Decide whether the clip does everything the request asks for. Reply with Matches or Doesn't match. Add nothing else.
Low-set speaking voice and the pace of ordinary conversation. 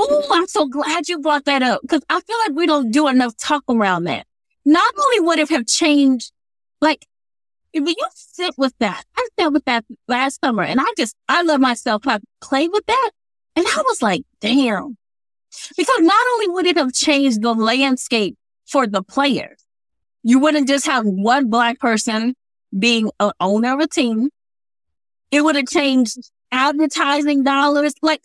Doesn't match